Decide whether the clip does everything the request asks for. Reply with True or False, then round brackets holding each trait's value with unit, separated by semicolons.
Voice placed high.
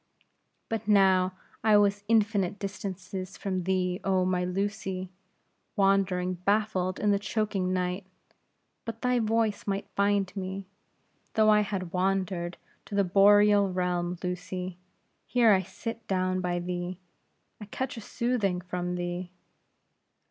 True (195 Hz)